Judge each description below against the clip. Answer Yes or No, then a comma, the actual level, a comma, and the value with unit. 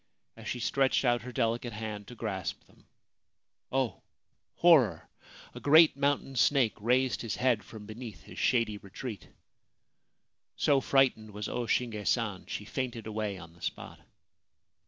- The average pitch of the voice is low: Yes, low, 115 Hz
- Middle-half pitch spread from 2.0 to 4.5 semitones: Yes, average, 3.6 semitones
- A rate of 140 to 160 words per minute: Yes, average, 155 wpm